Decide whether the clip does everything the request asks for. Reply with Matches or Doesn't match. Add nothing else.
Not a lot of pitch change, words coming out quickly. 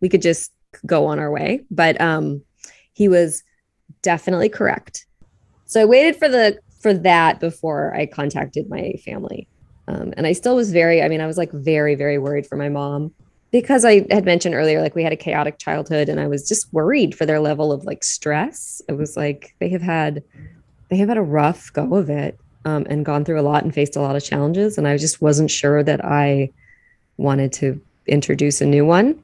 Doesn't match